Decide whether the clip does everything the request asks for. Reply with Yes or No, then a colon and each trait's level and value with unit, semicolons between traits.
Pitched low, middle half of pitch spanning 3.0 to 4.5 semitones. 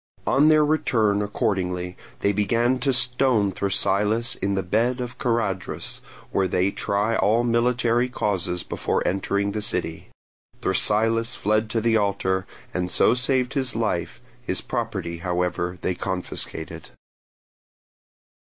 Yes: low, 105 Hz; average, 4.2 semitones